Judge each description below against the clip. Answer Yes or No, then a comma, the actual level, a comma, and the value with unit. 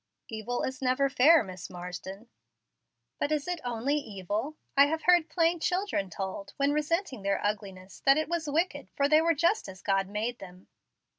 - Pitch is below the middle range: No, very high, 270 Hz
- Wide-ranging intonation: Yes, wide, 7.8 semitones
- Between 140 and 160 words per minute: No, average, 175 wpm